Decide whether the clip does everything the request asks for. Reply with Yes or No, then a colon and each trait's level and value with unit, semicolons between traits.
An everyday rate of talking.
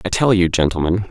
No: fast, 215 wpm